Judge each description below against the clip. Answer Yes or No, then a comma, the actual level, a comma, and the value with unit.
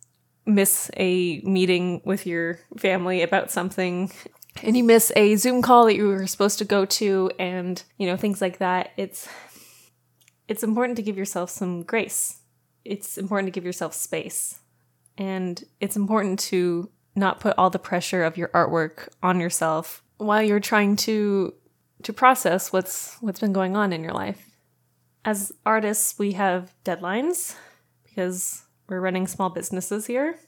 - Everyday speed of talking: Yes, average, 160 wpm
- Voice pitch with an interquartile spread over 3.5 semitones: No, narrow, 2.6 semitones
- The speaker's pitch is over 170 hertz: Yes, high, 190 Hz